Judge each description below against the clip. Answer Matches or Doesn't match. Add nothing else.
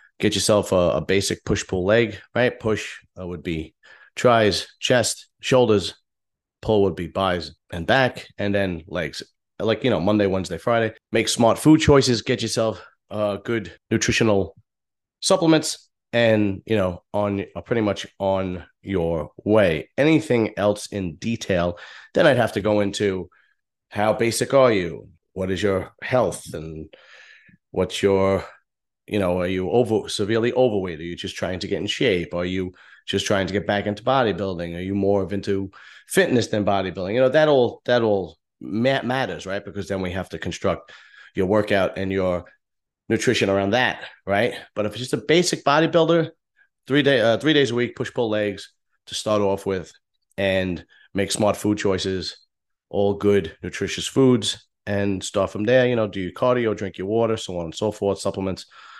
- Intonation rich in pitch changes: Doesn't match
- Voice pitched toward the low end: Matches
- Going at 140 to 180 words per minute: Matches